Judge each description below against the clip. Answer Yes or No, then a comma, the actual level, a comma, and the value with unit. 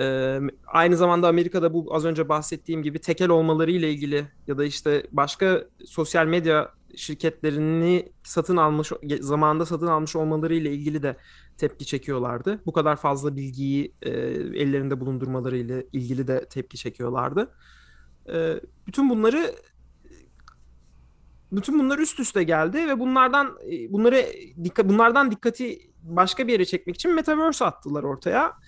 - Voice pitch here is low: No, medium, 160 Hz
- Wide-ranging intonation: No, average, 4.5 semitones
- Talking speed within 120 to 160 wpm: Yes, average, 135 wpm